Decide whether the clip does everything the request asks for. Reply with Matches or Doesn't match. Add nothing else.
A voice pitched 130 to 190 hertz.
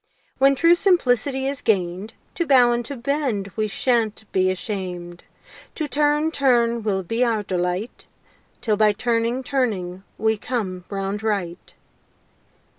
Doesn't match